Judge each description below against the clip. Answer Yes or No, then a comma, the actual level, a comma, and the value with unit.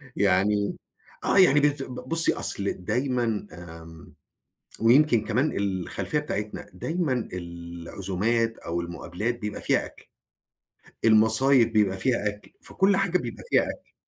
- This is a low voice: Yes, low, 110 Hz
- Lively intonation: Yes, wide, 5.7 semitones